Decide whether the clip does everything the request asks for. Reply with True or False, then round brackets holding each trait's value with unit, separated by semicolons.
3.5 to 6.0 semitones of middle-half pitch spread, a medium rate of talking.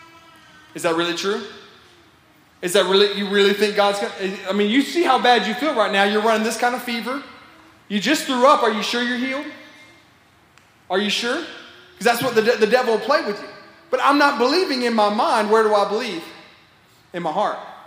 False (4.2 semitones; 215 wpm)